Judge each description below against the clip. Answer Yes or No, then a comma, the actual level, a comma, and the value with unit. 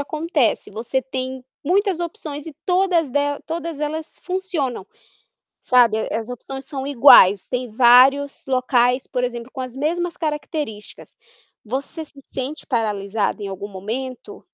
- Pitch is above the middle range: Yes, very high, 265 Hz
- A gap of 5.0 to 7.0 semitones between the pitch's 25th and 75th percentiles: No, average, 4.4 semitones